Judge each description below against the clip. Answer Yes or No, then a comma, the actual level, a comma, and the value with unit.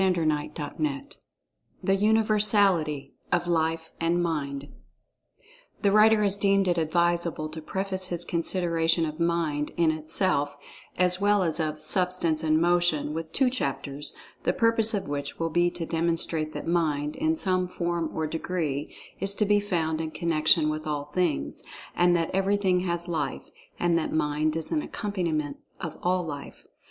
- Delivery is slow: No, average, 155 wpm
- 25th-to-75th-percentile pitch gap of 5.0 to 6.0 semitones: No, average, 3.2 semitones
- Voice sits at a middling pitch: Yes, medium, 170 Hz